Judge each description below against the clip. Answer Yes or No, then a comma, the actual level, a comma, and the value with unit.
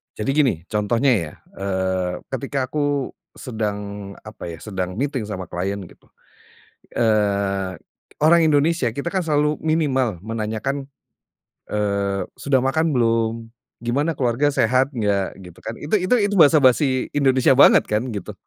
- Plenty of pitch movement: Yes, wide, 5.9 semitones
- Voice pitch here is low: Yes, low, 120 Hz